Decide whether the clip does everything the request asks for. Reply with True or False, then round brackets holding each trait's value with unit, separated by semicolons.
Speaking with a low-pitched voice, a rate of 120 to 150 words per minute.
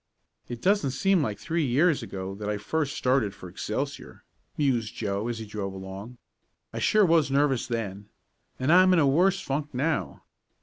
False (130 Hz; 175 wpm)